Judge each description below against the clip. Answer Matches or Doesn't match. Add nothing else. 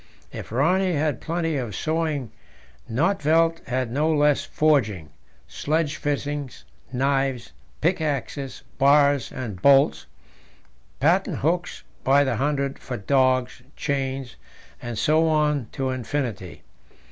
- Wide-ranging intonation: Doesn't match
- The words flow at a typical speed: Doesn't match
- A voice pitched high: Doesn't match